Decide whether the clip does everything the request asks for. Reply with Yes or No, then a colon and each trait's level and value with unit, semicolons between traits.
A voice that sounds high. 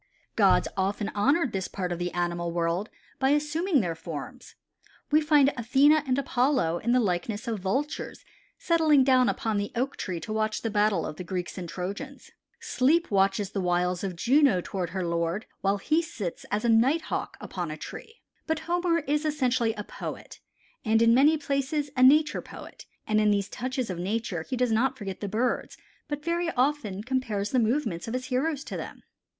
Yes: high, 230 Hz